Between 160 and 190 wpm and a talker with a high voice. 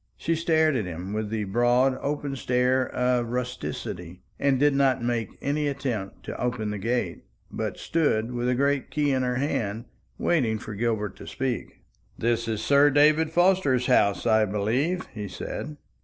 No: average, 170 wpm; low, 125 Hz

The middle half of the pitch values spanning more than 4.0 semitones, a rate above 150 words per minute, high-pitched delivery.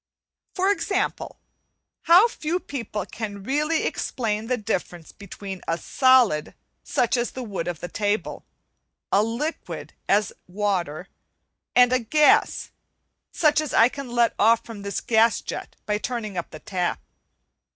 No: average, 4.5 semitones; average, 140 wpm; high, 225 Hz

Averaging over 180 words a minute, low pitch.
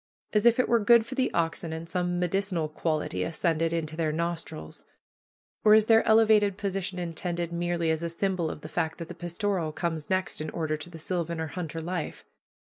No: average, 200 wpm; medium, 170 Hz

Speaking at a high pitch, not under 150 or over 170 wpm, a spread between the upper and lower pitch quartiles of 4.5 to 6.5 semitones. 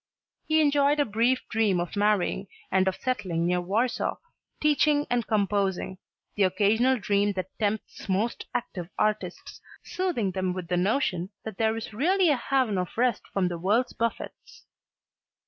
Yes: high, 210 Hz; average, 155 wpm; average, 5.0 semitones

